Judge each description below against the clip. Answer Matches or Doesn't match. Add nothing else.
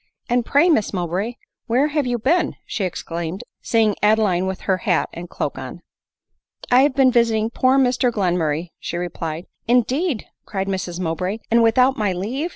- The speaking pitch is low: Doesn't match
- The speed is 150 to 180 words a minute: Doesn't match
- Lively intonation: Matches